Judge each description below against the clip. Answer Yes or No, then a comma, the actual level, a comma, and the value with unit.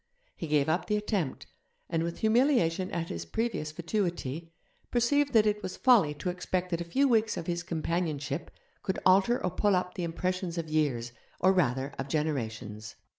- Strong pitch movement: No, average, 4.9 semitones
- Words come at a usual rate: Yes, average, 180 wpm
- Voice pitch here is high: No, medium, 175 Hz